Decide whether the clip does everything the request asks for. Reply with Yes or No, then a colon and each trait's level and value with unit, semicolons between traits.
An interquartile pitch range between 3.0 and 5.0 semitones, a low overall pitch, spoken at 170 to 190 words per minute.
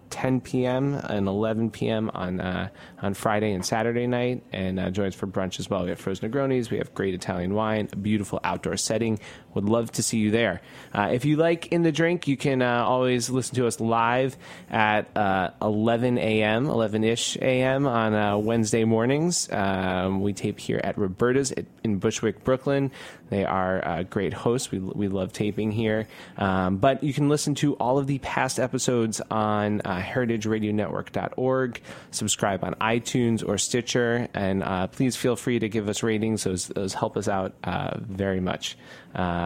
Yes: average, 4.1 semitones; low, 110 Hz; average, 185 wpm